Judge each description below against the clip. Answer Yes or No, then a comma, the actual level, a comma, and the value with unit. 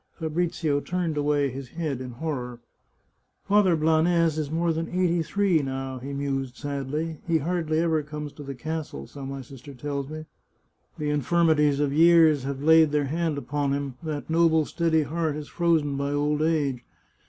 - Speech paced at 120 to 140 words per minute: No, average, 175 wpm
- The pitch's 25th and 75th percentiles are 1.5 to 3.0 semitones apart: Yes, narrow, 2.6 semitones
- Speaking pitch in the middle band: Yes, medium, 150 Hz